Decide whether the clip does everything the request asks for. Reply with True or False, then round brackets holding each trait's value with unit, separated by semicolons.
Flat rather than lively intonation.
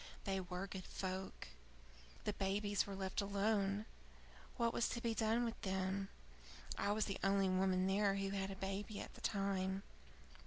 True (1.2 semitones)